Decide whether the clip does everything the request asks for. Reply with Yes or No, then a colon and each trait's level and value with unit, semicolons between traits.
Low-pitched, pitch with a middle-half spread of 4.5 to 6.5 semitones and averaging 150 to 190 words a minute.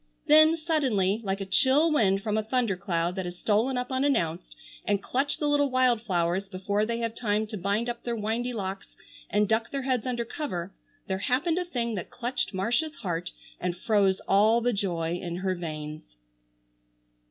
No: high, 215 Hz; average, 4.8 semitones; average, 185 wpm